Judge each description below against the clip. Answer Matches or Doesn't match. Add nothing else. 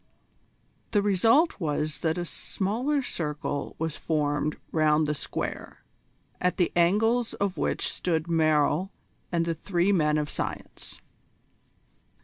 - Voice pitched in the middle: Matches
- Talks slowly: Matches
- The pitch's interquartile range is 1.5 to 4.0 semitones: Doesn't match